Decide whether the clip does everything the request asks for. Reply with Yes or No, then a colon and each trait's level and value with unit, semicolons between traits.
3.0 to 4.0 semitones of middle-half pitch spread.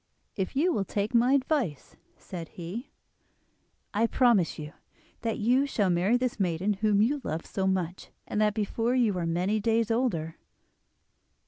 No: average, 4.7 semitones